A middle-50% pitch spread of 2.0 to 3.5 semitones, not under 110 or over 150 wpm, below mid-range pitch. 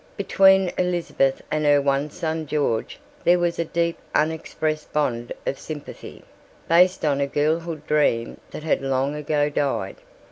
No: average, 2.9 semitones; average, 145 wpm; medium, 150 Hz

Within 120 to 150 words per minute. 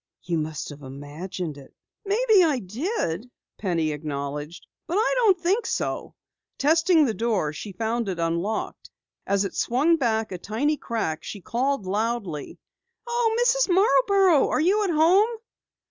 Yes: average, 145 wpm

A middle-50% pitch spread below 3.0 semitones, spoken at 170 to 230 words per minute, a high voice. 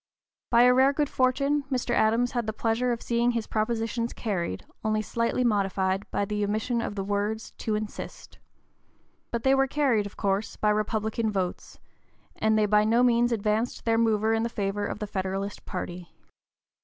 Yes: narrow, 2.5 semitones; average, 180 wpm; high, 220 Hz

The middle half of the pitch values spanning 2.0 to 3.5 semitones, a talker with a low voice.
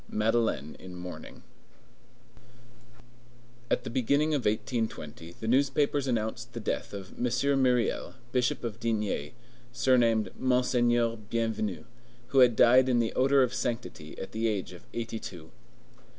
Yes: average, 2.8 semitones; low, 115 Hz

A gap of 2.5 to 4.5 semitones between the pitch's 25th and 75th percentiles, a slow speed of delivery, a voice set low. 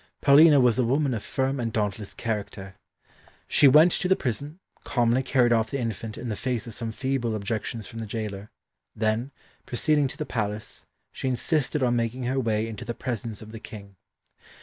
No: average, 3.4 semitones; average, 190 wpm; low, 120 Hz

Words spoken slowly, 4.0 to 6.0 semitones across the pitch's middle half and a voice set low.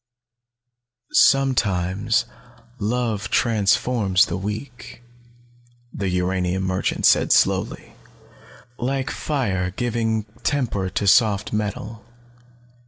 Yes: slow, 80 wpm; average, 4.3 semitones; low, 105 Hz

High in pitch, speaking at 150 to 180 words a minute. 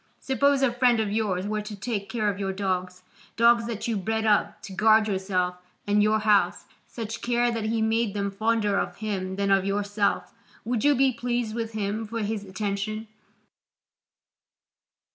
Yes: high, 215 Hz; average, 175 wpm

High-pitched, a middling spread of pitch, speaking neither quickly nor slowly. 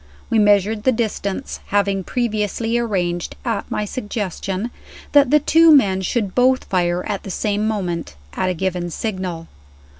Yes: high, 205 Hz; average, 3.8 semitones; average, 150 wpm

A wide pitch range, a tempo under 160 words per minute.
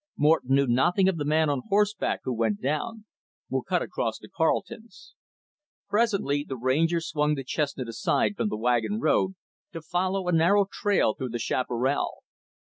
No: wide, 6.9 semitones; average, 165 wpm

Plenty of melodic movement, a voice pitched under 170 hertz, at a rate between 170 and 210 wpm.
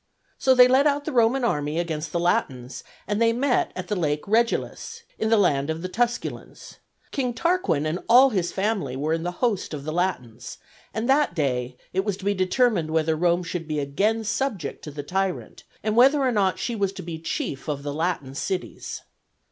No: wide, 7.0 semitones; medium, 185 Hz; fast, 205 wpm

